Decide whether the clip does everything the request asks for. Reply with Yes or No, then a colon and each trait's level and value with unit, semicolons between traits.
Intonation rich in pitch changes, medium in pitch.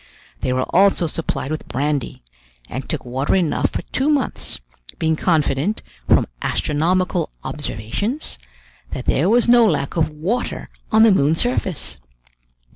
Yes: wide, 6.1 semitones; medium, 160 Hz